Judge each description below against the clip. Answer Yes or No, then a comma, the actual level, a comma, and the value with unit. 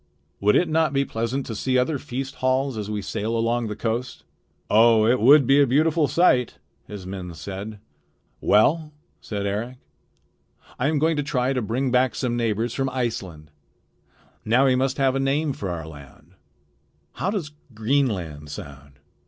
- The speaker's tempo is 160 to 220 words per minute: Yes, average, 170 wpm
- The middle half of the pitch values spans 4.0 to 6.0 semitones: Yes, average, 4.5 semitones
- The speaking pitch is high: No, low, 125 Hz